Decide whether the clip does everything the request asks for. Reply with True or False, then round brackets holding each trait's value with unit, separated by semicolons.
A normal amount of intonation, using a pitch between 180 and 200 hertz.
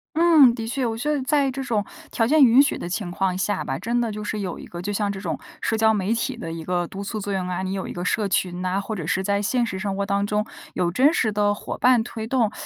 False (3.8 semitones; 210 Hz)